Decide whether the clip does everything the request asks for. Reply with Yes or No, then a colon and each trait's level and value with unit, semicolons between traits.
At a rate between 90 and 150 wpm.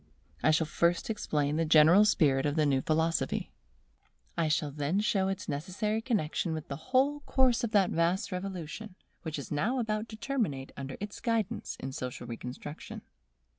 No: average, 170 wpm